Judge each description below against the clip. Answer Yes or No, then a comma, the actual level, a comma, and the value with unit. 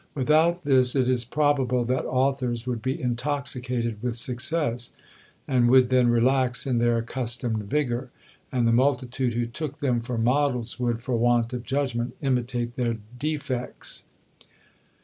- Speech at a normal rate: Yes, average, 145 wpm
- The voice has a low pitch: Yes, low, 125 Hz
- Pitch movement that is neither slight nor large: No, narrow, 1.9 semitones